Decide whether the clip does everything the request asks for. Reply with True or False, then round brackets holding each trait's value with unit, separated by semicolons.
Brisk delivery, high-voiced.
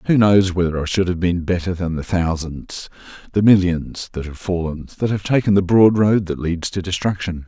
False (210 wpm; 90 Hz)